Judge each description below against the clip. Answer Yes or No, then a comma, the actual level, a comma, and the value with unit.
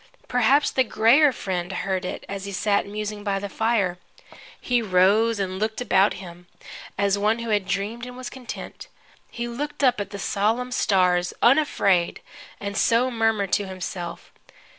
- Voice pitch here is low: No, high, 205 Hz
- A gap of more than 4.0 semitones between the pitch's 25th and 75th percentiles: No, average, 3.6 semitones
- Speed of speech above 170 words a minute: No, average, 160 wpm